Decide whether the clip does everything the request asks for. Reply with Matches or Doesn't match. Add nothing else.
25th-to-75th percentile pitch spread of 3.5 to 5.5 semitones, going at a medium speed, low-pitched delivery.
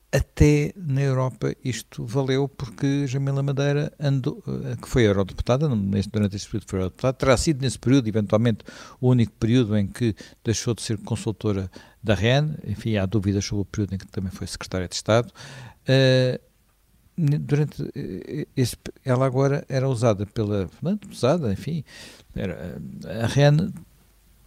Matches